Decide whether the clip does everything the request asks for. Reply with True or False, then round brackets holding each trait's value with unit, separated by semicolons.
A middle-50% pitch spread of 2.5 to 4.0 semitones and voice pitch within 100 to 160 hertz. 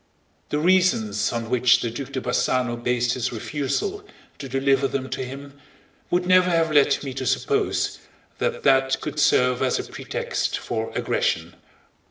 True (3.7 semitones; 135 Hz)